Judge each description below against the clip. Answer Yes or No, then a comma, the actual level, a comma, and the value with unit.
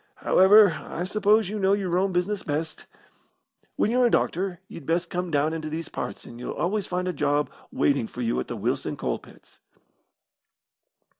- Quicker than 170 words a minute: Yes, average, 180 wpm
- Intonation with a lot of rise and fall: No, average, 4.2 semitones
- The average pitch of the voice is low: No, medium, 180 Hz